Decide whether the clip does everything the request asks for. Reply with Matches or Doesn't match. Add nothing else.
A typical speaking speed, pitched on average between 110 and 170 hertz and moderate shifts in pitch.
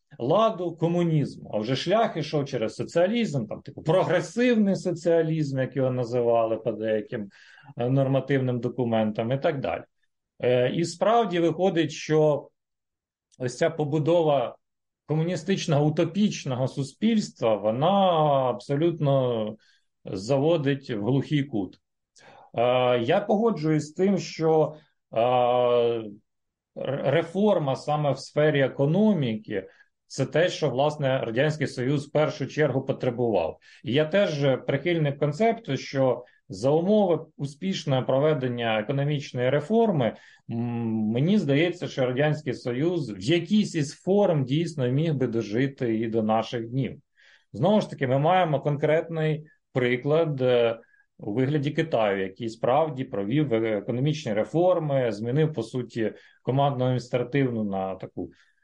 Matches